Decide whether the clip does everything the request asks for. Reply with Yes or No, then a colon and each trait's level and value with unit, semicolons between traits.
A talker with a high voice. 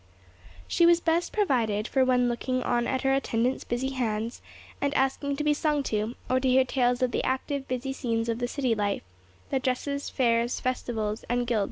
Yes: very high, 250 Hz